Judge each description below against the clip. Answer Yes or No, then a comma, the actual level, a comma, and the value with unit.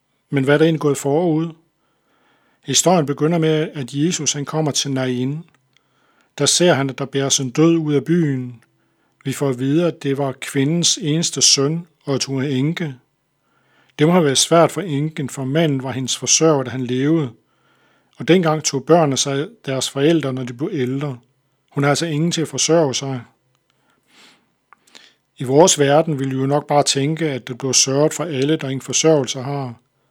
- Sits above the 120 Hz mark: Yes, medium, 140 Hz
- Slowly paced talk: No, average, 190 wpm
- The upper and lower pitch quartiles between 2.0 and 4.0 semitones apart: Yes, average, 2.9 semitones